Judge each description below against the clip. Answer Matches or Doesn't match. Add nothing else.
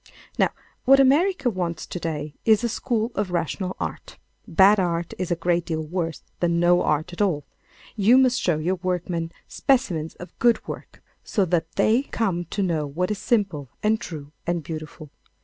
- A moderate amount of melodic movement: Matches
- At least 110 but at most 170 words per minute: Doesn't match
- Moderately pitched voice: Matches